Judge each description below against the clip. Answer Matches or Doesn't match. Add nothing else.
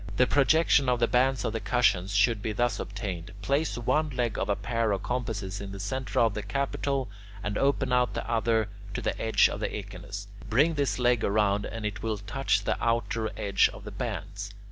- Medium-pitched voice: Doesn't match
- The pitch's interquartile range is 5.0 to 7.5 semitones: Doesn't match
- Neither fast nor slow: Doesn't match